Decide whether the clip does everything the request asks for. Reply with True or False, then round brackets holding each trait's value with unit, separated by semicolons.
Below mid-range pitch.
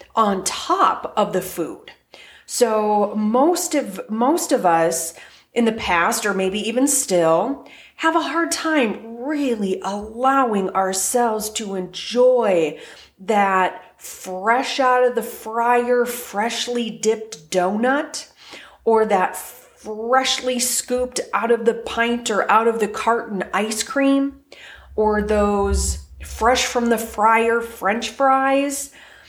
False (230 Hz)